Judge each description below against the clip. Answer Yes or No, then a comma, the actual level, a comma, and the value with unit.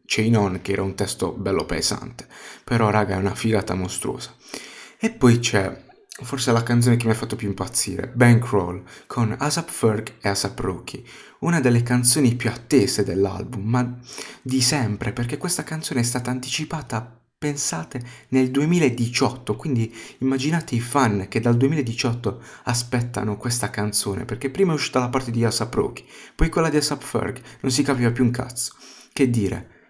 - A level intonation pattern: No, average, 3.8 semitones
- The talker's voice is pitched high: No, low, 120 Hz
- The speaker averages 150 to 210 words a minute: Yes, average, 165 wpm